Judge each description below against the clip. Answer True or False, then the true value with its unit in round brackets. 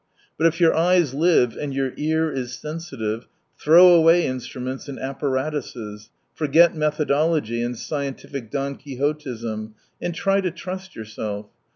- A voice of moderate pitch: True (145 Hz)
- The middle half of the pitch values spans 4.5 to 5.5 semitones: True (4.8 semitones)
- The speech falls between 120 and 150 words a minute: True (135 wpm)